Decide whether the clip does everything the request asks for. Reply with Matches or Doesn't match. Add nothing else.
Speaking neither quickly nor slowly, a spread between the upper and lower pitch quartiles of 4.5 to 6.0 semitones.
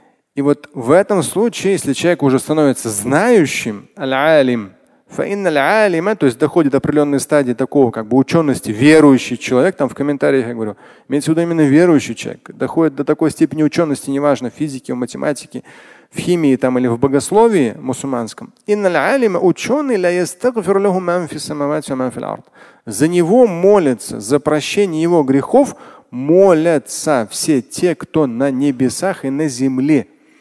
Matches